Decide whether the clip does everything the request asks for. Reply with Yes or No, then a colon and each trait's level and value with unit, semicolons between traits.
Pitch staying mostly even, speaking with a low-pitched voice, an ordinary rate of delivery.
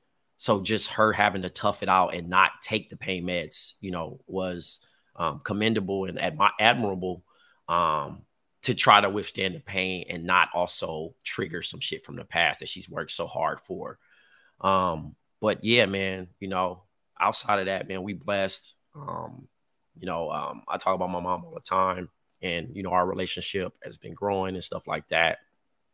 Yes: narrow, 1.4 semitones; very low, 95 Hz; average, 185 wpm